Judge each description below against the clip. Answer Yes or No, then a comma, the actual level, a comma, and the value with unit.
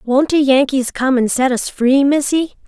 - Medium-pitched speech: No, very high, 270 Hz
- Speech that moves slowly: No, average, 200 wpm